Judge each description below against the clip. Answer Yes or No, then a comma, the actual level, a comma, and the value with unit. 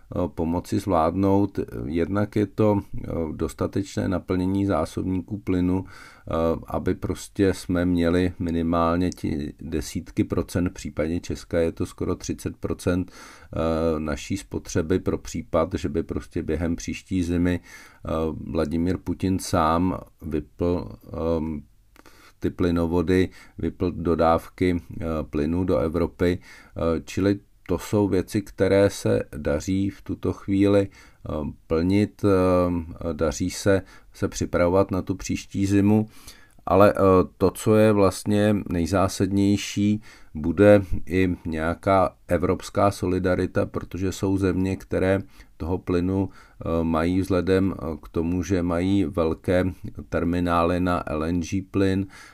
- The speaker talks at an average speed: No, slow, 105 wpm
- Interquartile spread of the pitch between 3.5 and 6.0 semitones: No, average, 2.8 semitones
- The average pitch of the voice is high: No, very low, 90 Hz